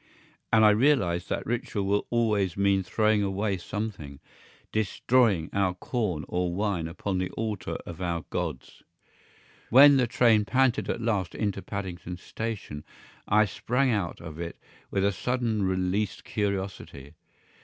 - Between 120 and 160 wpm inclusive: Yes, average, 140 wpm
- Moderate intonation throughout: Yes, average, 3.6 semitones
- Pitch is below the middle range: Yes, low, 100 Hz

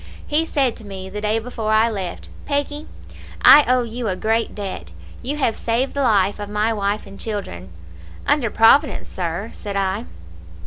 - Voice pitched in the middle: No, high, 220 Hz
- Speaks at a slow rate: No, average, 175 wpm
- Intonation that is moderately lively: Yes, average, 3.8 semitones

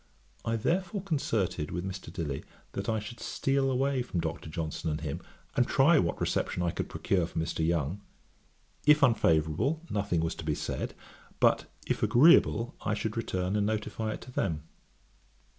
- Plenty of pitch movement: Yes, wide, 7.2 semitones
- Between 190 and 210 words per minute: No, average, 170 wpm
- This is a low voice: Yes, low, 105 Hz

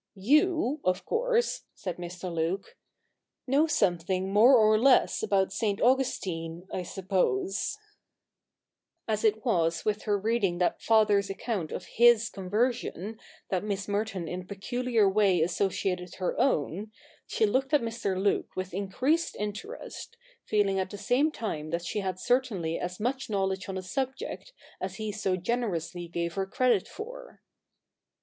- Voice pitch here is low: No, high, 205 Hz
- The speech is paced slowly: No, average, 145 wpm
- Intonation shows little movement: No, average, 4.6 semitones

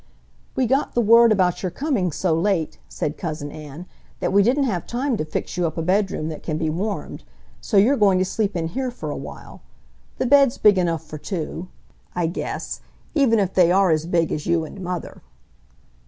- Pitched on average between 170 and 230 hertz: Yes, medium, 185 Hz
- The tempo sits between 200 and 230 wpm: Yes, fast, 205 wpm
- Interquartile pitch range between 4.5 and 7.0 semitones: Yes, average, 5.2 semitones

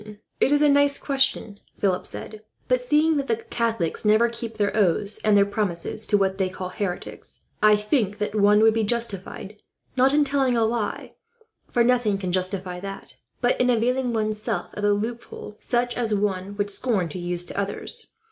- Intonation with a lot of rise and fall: No, average, 3.3 semitones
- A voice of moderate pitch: No, high, 215 Hz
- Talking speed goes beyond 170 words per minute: Yes, average, 190 wpm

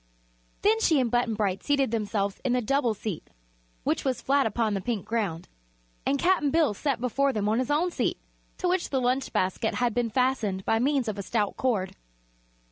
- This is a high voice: Yes, high, 240 Hz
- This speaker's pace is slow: No, average, 200 wpm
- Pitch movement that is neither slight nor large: Yes, average, 4.6 semitones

